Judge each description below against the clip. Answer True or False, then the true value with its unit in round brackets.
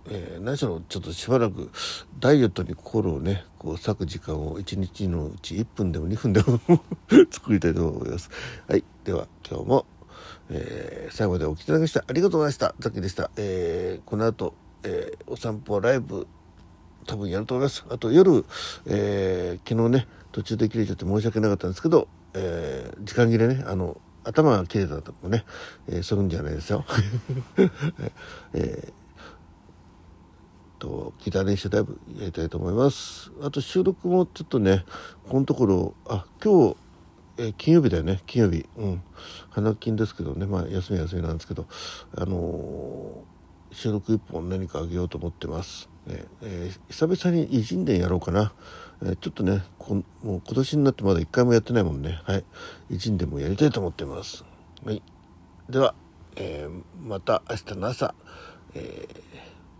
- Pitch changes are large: False (4.7 semitones)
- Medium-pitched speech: False (95 Hz)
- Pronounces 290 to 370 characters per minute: True (325 characters per minute)